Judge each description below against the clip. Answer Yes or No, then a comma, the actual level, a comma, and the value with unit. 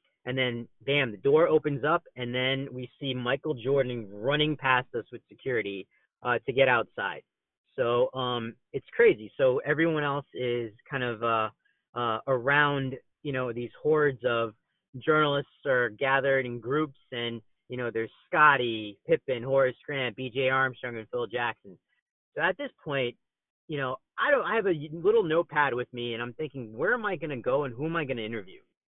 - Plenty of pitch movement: No, average, 3.7 semitones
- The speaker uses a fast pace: No, average, 185 wpm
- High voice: No, low, 130 Hz